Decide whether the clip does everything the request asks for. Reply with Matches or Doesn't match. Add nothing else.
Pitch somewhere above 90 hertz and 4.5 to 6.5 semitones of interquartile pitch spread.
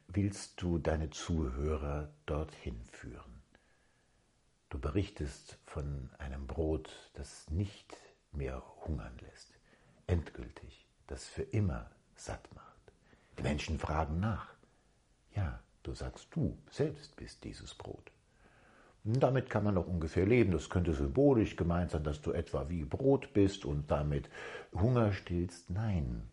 Doesn't match